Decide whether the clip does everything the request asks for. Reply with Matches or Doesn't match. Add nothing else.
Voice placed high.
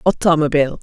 Doesn't match